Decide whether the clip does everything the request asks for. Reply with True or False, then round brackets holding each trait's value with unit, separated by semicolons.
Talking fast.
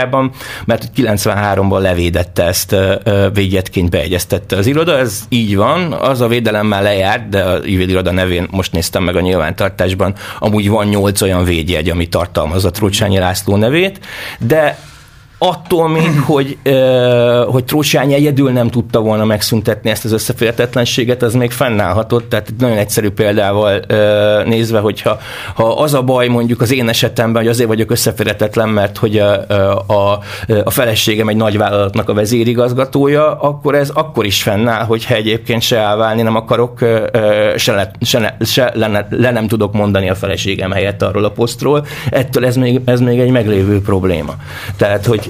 True (160 wpm)